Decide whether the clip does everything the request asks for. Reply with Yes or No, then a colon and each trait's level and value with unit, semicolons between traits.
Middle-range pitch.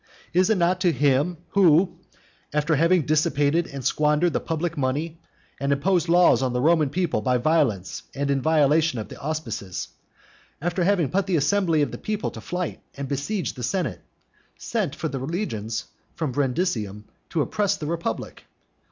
Yes: medium, 155 Hz